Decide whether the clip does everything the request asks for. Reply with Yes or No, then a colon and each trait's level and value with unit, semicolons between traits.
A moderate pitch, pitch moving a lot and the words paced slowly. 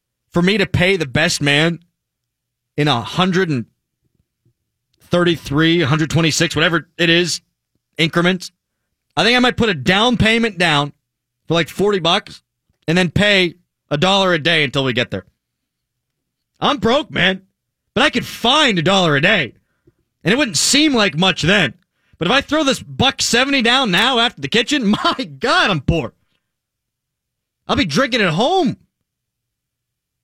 No: medium, 170 Hz; wide, 6.0 semitones; average, 165 wpm